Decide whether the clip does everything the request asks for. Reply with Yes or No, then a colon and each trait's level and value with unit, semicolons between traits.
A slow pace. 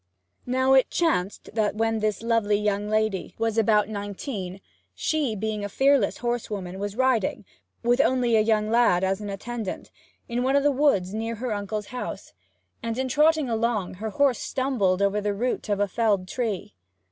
No: average, 175 wpm